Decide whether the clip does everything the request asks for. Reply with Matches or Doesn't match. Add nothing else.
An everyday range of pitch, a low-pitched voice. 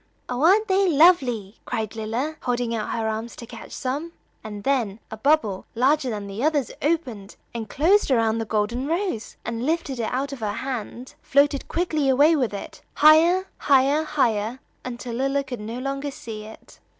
Doesn't match